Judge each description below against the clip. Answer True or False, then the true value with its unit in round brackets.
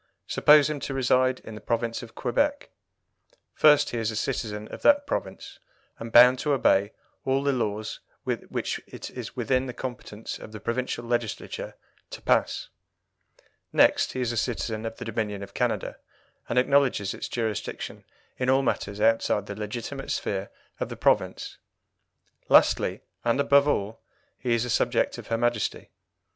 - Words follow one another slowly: False (160 wpm)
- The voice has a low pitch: True (120 Hz)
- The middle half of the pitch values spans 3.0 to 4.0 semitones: True (3.4 semitones)